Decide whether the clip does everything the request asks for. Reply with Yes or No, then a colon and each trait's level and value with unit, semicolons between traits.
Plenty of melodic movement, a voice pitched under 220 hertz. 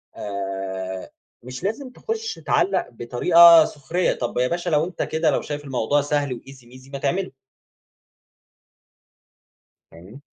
Yes: wide, 6.2 semitones; medium, 140 Hz